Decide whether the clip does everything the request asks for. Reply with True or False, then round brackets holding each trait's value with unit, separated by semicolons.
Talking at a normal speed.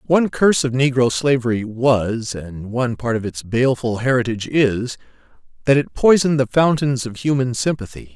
True (160 wpm)